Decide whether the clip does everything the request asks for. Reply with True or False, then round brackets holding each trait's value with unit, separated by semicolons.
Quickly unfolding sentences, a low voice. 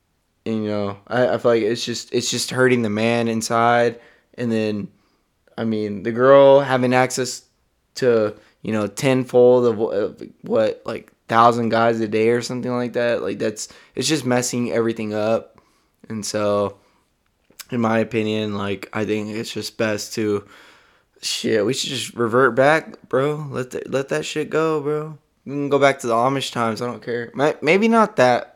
False (180 wpm; 120 Hz)